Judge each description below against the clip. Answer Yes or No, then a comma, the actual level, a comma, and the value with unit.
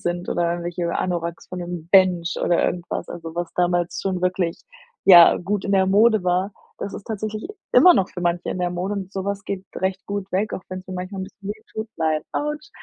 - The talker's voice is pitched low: No, medium, 185 Hz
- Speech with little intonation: Yes, narrow, 2.2 semitones